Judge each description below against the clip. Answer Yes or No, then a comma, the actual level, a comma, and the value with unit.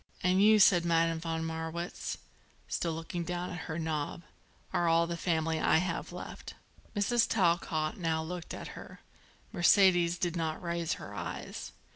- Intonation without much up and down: Yes, narrow, 1.5 semitones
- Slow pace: No, average, 155 wpm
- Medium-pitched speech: Yes, medium, 170 Hz